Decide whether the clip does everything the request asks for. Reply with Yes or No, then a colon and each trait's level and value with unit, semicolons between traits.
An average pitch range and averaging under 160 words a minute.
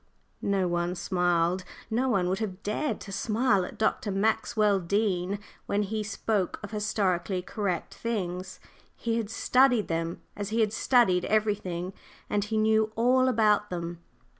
Yes: average, 3.2 semitones; average, 150 wpm